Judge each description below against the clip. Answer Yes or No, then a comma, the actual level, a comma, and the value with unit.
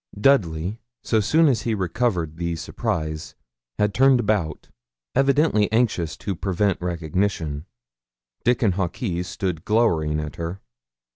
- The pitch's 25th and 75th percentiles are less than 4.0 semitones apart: No, average, 5.3 semitones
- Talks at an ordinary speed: No, slow, 120 wpm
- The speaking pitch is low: Yes, very low, 95 Hz